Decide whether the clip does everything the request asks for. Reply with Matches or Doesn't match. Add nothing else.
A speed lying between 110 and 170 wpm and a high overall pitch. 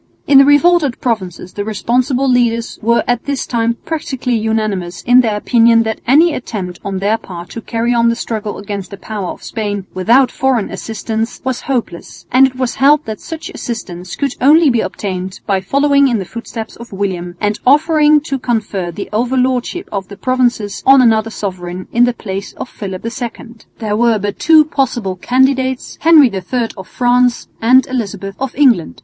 Doesn't match